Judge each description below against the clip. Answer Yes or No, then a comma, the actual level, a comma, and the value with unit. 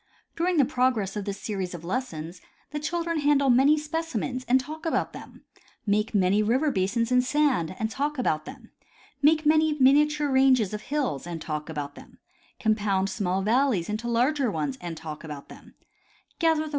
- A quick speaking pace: No, average, 175 wpm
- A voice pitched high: Yes, high, 245 Hz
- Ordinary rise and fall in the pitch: No, wide, 7.6 semitones